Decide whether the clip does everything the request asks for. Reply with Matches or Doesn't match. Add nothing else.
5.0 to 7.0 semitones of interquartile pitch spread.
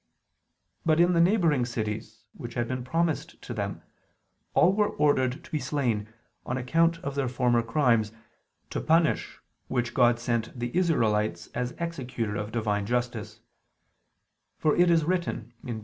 Matches